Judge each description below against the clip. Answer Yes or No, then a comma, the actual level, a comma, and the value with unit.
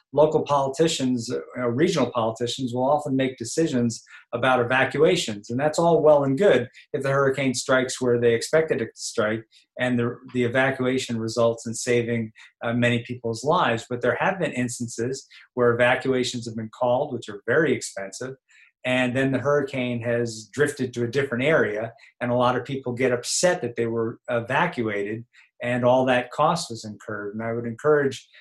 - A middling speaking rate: Yes, average, 175 wpm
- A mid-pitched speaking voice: No, low, 125 Hz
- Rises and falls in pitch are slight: Yes, narrow, 2.3 semitones